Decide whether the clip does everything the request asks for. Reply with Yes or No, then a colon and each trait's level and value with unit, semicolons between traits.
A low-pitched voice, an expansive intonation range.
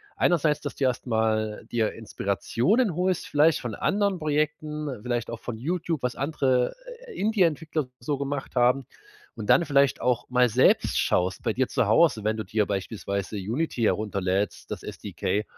Yes: low, 125 Hz; wide, 5.8 semitones